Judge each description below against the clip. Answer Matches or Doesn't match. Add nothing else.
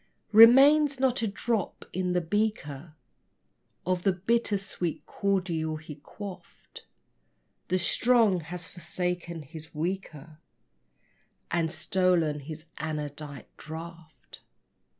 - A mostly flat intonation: Doesn't match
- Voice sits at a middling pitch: Matches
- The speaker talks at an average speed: Doesn't match